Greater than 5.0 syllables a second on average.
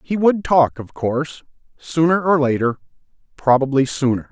No: 4.8 syllables/s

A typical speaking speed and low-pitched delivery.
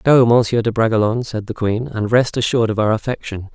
No: fast, 220 wpm; low, 115 Hz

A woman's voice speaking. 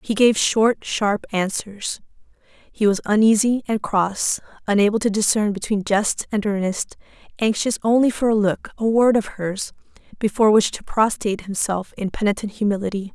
Yes: female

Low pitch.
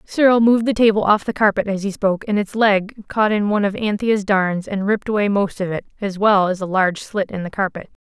No: high, 205 Hz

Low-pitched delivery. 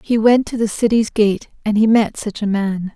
No: high, 215 Hz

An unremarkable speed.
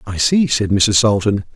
Yes: average, 195 wpm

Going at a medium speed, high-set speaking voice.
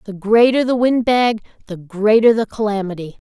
Yes: average, 165 wpm; high, 215 Hz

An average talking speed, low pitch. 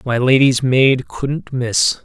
Yes: average, 145 wpm; low, 125 Hz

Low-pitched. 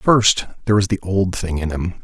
Yes: very low, 95 Hz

